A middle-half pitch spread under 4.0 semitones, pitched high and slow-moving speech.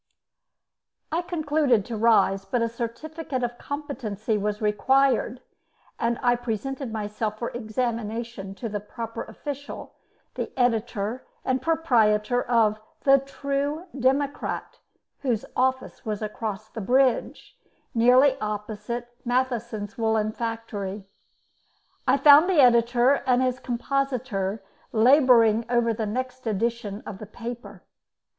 Yes: average, 3.3 semitones; high, 235 Hz; slow, 115 wpm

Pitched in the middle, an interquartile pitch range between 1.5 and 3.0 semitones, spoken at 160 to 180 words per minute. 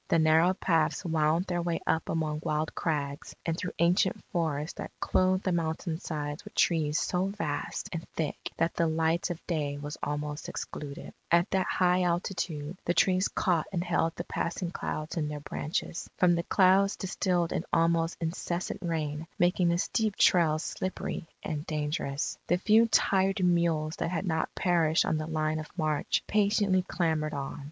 Yes: medium, 165 Hz; average, 2.7 semitones; average, 170 wpm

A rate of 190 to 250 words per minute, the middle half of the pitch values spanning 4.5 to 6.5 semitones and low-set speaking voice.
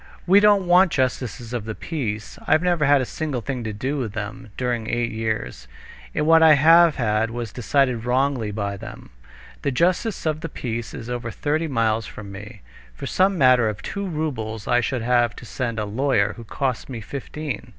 Yes: average, 195 wpm; average, 5.3 semitones; low, 125 Hz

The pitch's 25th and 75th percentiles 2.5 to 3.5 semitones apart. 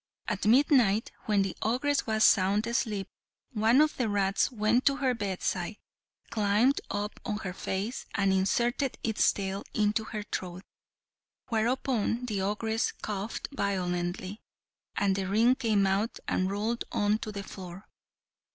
Yes: average, 3.0 semitones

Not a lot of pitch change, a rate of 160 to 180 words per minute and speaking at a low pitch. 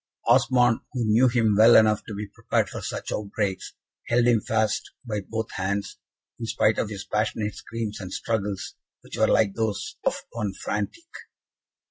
Yes: narrow, 2.0 semitones; average, 165 wpm; low, 110 Hz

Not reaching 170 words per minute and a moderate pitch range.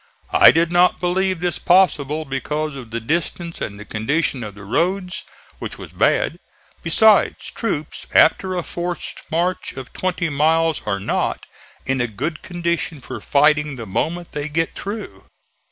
Yes: average, 155 wpm; average, 4.7 semitones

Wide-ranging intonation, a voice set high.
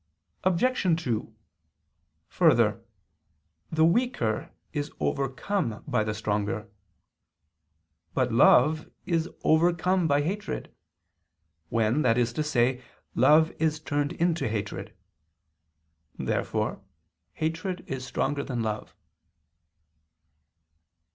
No: wide, 6.0 semitones; medium, 145 Hz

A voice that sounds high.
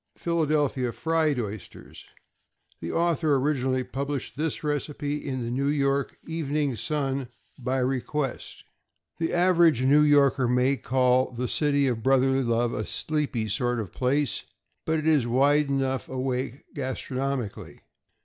No: low, 135 Hz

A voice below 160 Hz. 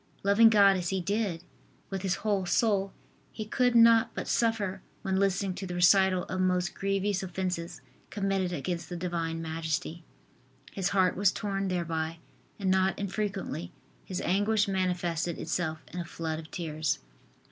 No: medium, 185 Hz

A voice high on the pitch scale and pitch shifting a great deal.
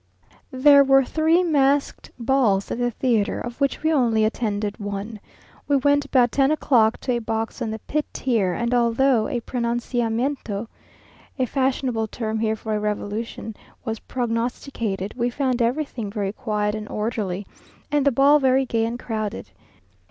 No: high, 235 Hz; average, 3.6 semitones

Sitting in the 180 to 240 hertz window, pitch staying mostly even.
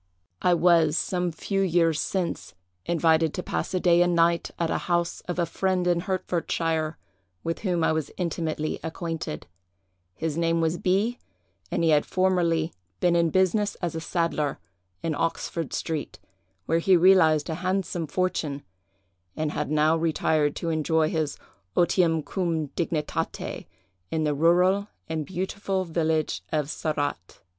No: medium, 165 Hz; narrow, 2.2 semitones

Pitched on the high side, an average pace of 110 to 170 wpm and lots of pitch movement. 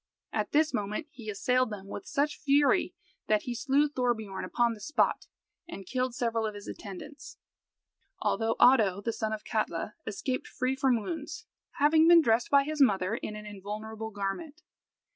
No: high, 235 Hz; average, 165 wpm; average, 4.9 semitones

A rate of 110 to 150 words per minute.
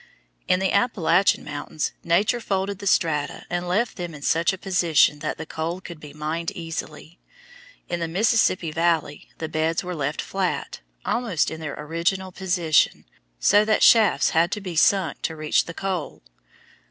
No: average, 165 wpm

